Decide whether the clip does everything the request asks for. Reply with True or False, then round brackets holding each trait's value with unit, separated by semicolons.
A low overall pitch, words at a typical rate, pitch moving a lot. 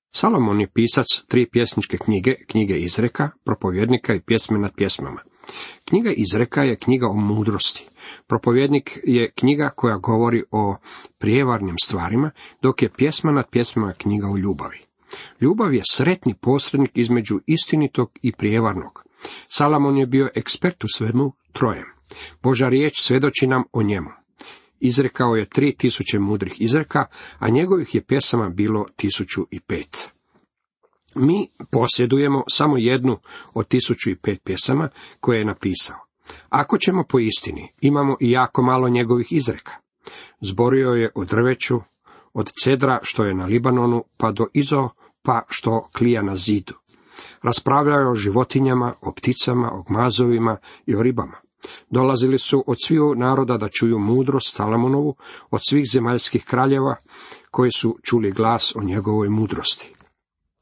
False (120 Hz; 140 wpm; 3.6 semitones)